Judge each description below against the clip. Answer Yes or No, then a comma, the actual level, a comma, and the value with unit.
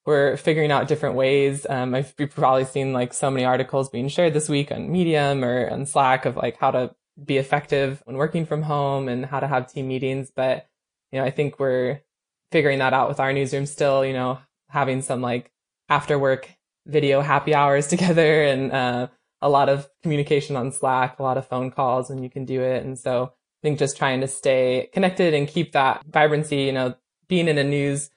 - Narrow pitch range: Yes, narrow, 1.9 semitones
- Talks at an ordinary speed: No, fast, 210 wpm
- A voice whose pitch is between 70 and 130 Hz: No, medium, 140 Hz